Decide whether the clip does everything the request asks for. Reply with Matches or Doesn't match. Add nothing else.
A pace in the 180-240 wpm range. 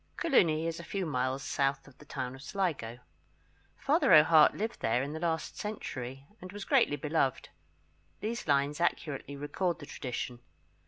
Doesn't match